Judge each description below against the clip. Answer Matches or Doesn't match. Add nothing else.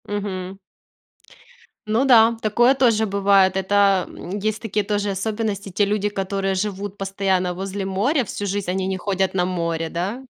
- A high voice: Matches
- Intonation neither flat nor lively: Doesn't match